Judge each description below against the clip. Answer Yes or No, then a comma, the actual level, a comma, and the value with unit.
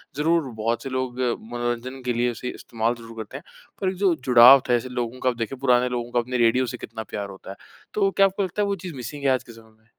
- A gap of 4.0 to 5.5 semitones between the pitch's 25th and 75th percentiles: No, narrow, 2.5 semitones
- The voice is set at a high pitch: No, low, 125 Hz